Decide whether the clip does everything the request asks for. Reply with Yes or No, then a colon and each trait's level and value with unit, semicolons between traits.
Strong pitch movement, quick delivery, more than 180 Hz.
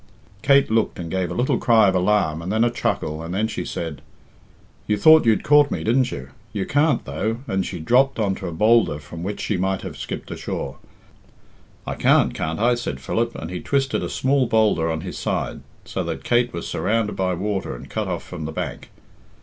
No: wide, 5.8 semitones; fast, 215 wpm; low, 105 Hz